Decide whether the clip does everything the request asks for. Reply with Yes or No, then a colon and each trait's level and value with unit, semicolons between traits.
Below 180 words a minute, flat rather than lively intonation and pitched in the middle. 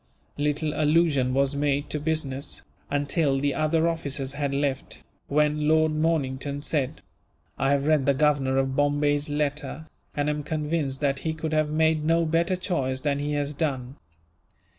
Yes: average, 160 wpm; narrow, 1.9 semitones; medium, 145 Hz